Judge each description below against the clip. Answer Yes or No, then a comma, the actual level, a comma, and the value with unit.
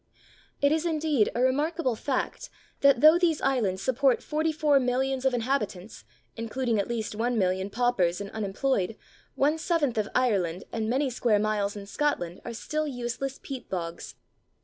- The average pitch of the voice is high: Yes, high, 245 Hz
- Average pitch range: Yes, average, 5.0 semitones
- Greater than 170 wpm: No, average, 150 wpm